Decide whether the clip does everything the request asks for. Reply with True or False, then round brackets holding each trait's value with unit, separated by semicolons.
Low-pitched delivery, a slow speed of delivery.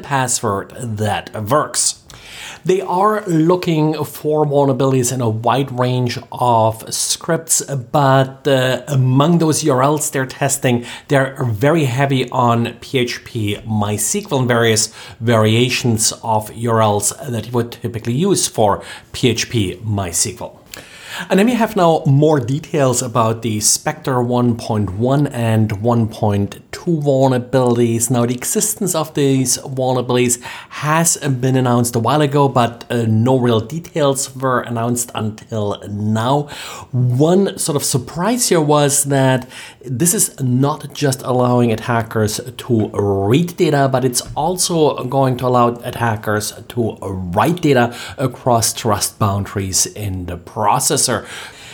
True (125 Hz; 125 wpm)